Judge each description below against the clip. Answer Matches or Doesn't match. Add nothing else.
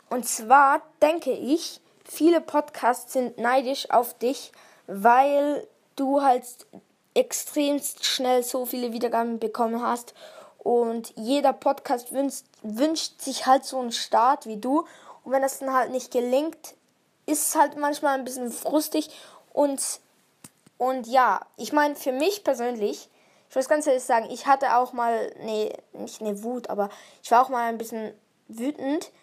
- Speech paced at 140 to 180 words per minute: Matches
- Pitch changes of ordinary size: Matches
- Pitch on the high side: Matches